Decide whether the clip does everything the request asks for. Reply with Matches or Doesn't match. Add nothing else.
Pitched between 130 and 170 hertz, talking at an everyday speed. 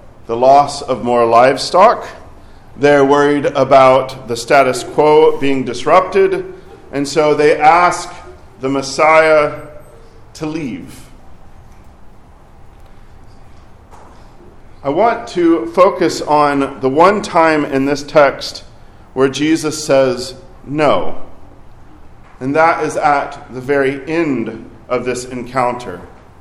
Doesn't match